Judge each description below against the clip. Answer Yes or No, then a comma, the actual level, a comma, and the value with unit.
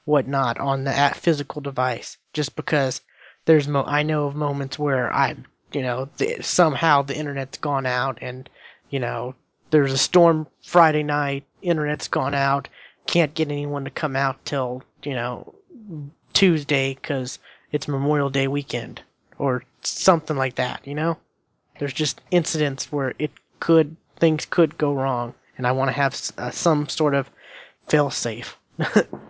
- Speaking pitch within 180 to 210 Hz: No, medium, 140 Hz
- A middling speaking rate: Yes, average, 160 wpm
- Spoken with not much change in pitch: Yes, narrow, 2.2 semitones